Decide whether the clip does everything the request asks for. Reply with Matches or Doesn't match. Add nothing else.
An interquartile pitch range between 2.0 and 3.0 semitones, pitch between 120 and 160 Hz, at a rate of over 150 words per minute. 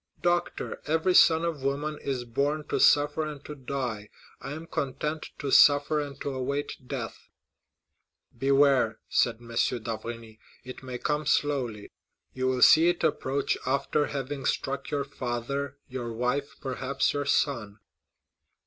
Doesn't match